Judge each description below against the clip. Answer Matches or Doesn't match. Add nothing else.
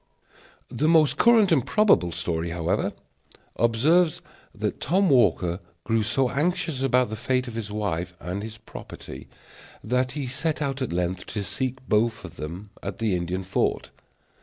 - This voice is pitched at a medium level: Doesn't match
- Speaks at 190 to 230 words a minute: Doesn't match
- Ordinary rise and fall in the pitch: Doesn't match